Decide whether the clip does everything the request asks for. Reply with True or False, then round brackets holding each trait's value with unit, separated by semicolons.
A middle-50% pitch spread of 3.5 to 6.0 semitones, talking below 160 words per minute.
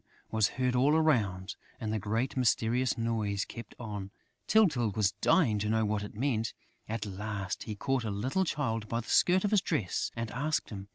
False (3.9 semitones; 190 wpm)